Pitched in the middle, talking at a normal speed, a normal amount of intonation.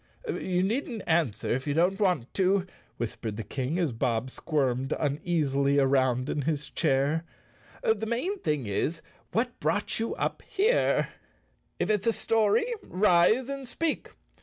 No: medium, 165 Hz; average, 155 wpm; wide, 8.1 semitones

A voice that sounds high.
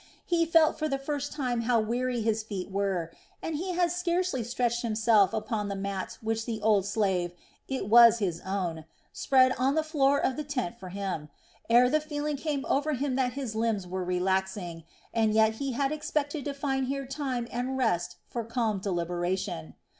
Yes: high, 235 Hz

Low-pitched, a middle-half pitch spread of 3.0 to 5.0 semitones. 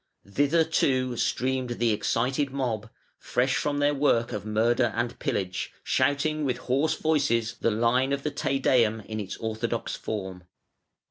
Yes: low, 125 Hz; average, 3.9 semitones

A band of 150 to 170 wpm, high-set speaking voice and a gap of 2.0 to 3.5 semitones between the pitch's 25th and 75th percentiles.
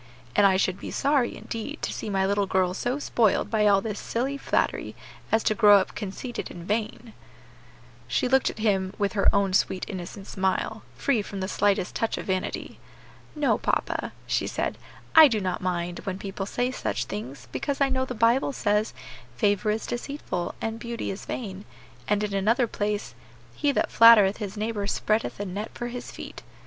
No: average, 185 wpm; high, 210 Hz; average, 3.2 semitones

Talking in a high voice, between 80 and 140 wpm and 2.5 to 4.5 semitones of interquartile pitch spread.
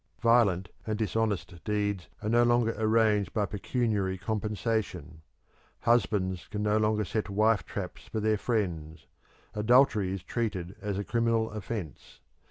No: low, 105 Hz; slow, 135 wpm; average, 2.8 semitones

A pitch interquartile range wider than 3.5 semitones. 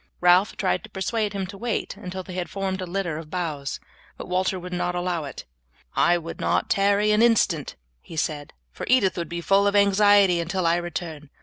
No: narrow, 2.6 semitones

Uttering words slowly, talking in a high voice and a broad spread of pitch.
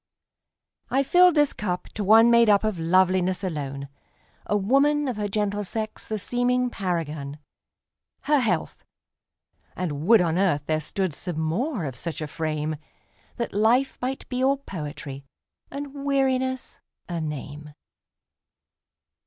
Yes: slow, 130 wpm; high, 195 Hz; wide, 8.0 semitones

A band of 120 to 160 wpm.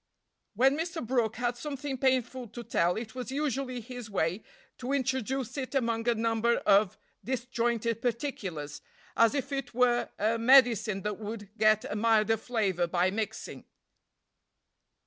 Yes: average, 145 wpm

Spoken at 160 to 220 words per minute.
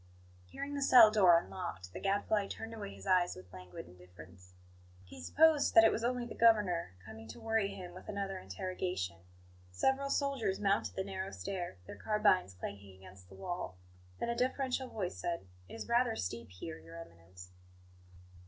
Yes: average, 170 wpm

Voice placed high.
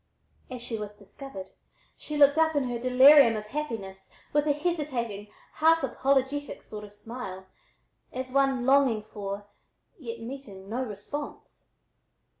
Yes: very high, 250 Hz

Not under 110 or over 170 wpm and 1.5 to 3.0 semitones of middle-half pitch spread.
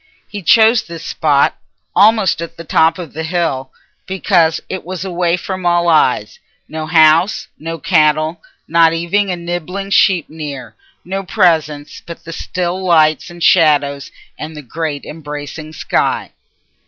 Yes: average, 140 wpm; average, 2.7 semitones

